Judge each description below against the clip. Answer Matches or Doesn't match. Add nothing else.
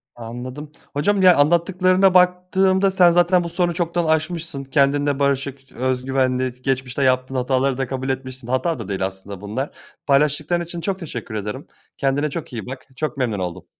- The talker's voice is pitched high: Doesn't match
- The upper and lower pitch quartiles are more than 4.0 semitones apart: Matches